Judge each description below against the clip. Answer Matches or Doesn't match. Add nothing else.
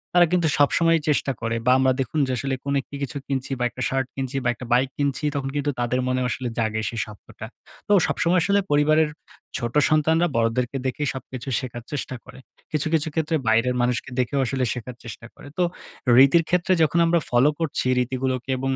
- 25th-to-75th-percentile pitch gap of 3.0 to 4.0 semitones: Matches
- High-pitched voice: Doesn't match